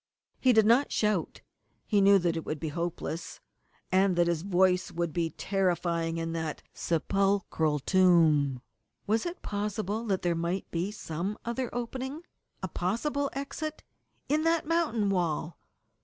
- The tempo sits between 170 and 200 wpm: No, average, 145 wpm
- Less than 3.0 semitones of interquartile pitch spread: No, average, 5.0 semitones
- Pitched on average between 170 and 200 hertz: Yes, high, 190 Hz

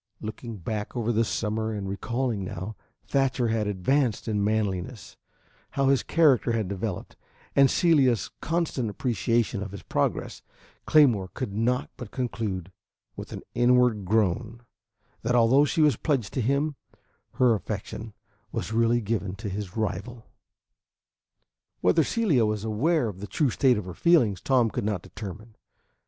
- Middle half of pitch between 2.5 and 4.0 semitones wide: Yes, average, 3.7 semitones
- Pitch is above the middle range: No, low, 115 Hz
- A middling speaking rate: Yes, average, 145 wpm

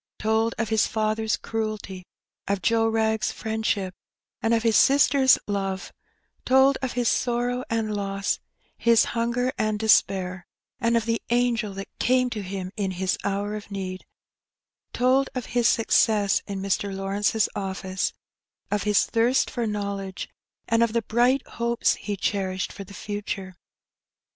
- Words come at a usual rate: Yes, average, 155 wpm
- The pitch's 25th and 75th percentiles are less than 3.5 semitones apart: Yes, average, 2.9 semitones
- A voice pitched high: Yes, high, 215 Hz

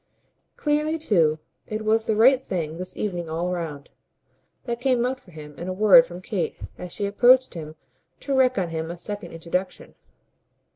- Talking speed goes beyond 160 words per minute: Yes, average, 180 wpm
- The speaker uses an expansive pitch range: Yes, wide, 6.5 semitones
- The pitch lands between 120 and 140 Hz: No, high, 195 Hz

